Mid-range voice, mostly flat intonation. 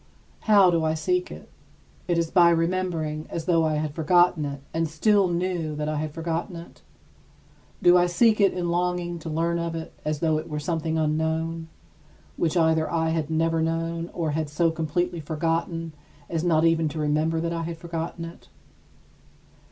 Yes: medium, 165 Hz; narrow, 1.4 semitones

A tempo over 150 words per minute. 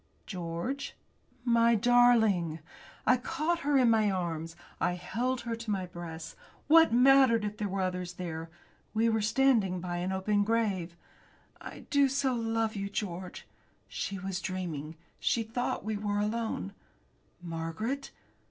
No: average, 145 wpm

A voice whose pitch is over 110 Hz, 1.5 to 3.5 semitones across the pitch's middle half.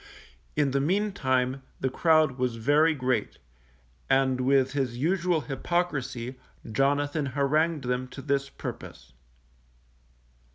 Yes: medium, 140 Hz; average, 3.1 semitones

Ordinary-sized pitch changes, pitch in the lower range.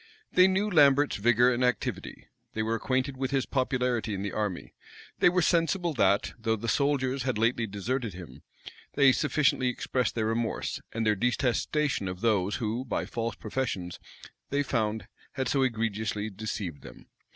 Yes: average, 3.8 semitones; low, 120 Hz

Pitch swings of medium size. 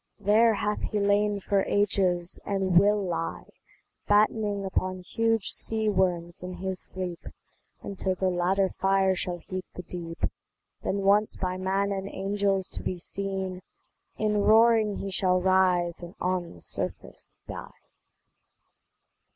No: narrow, 1.9 semitones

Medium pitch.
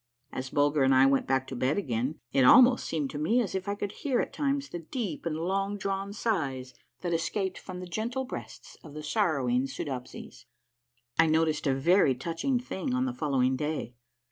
Yes: medium, 165 Hz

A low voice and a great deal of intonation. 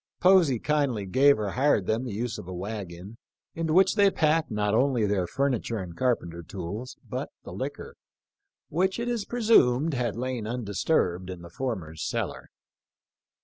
Yes: low, 120 Hz; wide, 6.9 semitones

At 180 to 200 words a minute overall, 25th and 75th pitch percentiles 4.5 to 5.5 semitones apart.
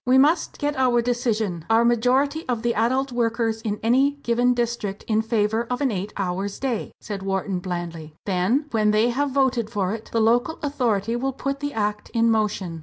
No: average, 190 wpm; average, 3.3 semitones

